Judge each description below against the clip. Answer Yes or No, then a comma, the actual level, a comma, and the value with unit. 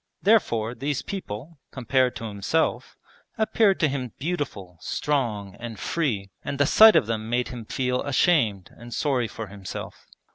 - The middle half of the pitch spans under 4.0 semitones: No, average, 5.3 semitones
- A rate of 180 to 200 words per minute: No, average, 150 wpm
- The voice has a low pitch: Yes, low, 125 Hz